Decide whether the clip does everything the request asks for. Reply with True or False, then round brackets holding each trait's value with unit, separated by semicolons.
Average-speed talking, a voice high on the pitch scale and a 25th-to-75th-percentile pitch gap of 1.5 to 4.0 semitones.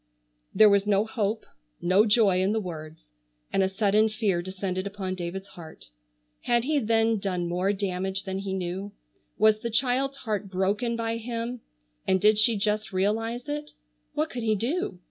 True (170 wpm; 205 Hz; 3.1 semitones)